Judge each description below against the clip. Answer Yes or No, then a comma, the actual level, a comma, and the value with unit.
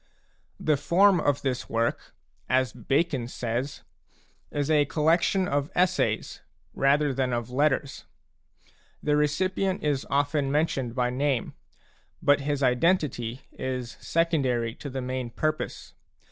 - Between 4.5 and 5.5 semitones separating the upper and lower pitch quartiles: No, average, 3.2 semitones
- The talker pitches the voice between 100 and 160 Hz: Yes, medium, 140 Hz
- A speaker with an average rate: No, slow, 125 wpm